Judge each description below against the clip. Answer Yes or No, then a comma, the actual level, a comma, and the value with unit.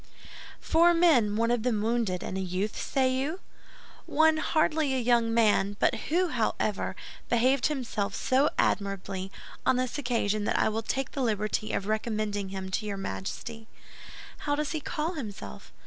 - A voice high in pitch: Yes, high, 230 Hz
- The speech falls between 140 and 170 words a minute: Yes, average, 165 wpm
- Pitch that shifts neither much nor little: Yes, average, 5.0 semitones